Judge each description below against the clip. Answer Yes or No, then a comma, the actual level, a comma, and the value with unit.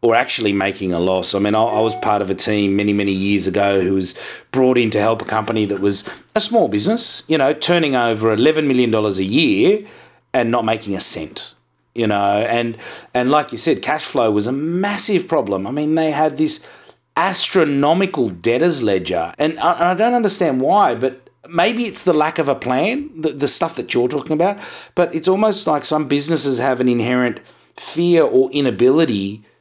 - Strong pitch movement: Yes, wide, 7.2 semitones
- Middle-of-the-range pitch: No, low, 125 Hz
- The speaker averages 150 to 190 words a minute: No, fast, 205 wpm